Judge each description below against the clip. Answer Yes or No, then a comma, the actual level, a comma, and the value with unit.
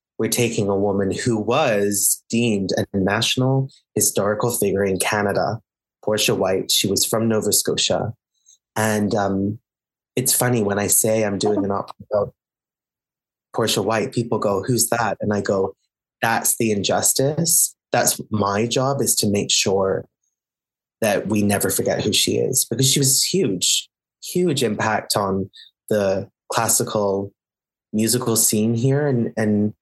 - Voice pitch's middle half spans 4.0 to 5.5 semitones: No, average, 3.0 semitones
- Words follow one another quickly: No, average, 145 wpm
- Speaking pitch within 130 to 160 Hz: No, low, 110 Hz